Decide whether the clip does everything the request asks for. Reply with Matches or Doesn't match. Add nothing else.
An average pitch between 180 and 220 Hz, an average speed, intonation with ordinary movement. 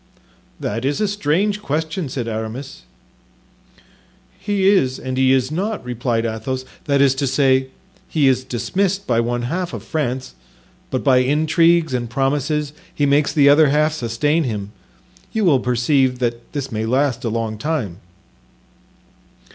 Doesn't match